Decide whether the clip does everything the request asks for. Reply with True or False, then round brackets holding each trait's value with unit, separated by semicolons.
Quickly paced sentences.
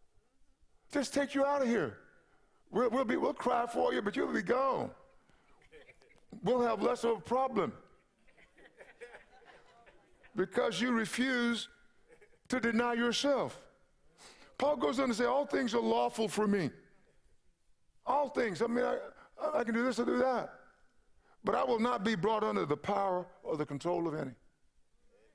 False (155 wpm)